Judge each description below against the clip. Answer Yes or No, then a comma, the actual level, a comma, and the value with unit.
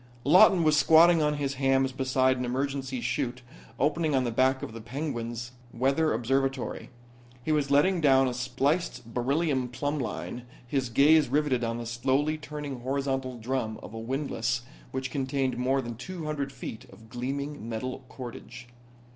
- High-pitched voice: No, low, 135 Hz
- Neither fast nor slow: Yes, average, 160 wpm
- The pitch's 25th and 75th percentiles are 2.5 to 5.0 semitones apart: Yes, average, 2.9 semitones